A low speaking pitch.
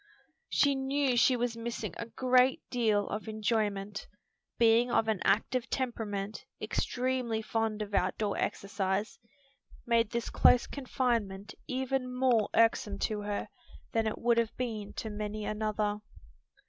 No: high, 225 Hz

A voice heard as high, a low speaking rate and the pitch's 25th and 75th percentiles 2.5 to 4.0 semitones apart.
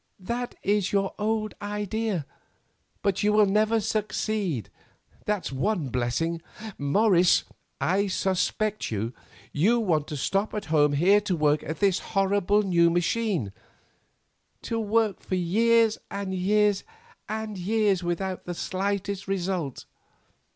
Yes: high, 195 Hz; slow, 125 wpm; average, 3.5 semitones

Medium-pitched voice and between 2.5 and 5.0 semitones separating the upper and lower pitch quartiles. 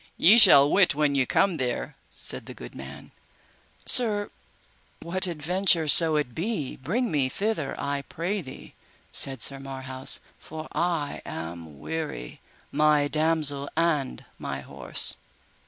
Yes: medium, 150 Hz; average, 4.3 semitones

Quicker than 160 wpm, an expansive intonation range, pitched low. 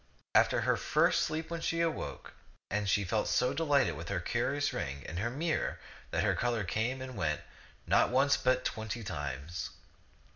Yes: average, 170 wpm; wide, 7.4 semitones; low, 120 Hz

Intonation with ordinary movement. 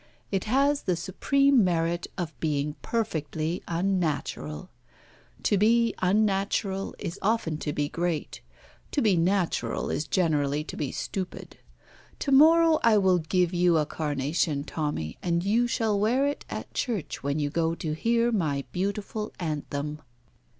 No: wide, 5.7 semitones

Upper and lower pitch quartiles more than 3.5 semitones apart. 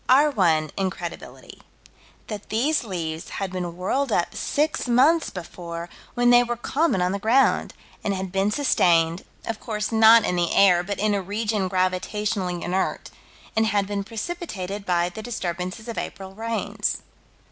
Yes: average, 4.1 semitones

